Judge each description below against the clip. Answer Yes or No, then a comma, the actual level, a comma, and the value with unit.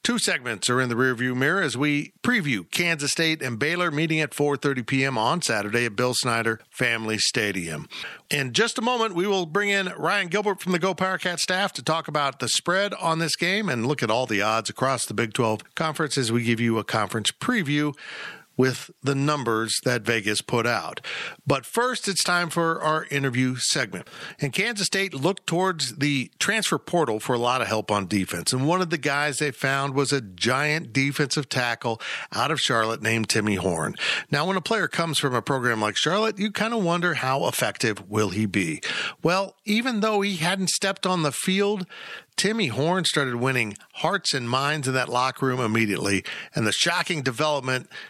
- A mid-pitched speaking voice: Yes, medium, 145 Hz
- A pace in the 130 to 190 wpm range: No, average, 200 wpm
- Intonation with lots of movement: Yes, wide, 6.6 semitones